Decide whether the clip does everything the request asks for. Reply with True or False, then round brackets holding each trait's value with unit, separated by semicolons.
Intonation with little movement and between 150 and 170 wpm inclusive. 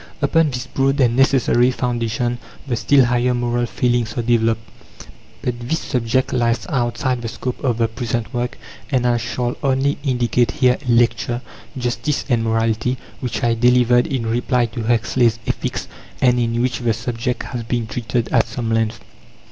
True (1.5 semitones; 165 wpm)